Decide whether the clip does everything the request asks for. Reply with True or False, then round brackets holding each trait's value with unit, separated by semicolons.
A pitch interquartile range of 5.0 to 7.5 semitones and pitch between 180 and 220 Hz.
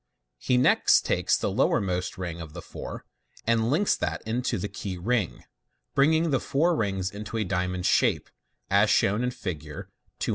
False (5.5 semitones; 105 Hz)